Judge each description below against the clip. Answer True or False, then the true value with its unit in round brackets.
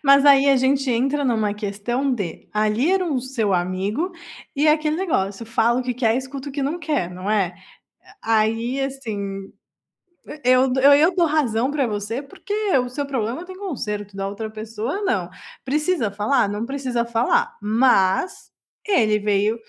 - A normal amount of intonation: True (4.9 semitones)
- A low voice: False (245 Hz)